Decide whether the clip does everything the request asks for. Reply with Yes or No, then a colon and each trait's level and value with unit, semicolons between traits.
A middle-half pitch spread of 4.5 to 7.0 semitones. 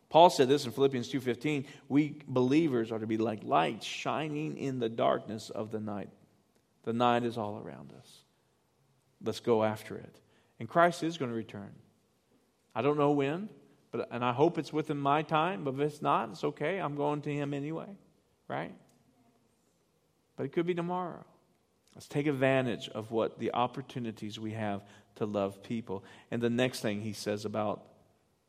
Yes: average, 5.1 semitones